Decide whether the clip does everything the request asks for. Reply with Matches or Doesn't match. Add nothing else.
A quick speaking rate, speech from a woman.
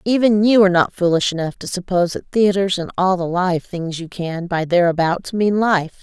Matches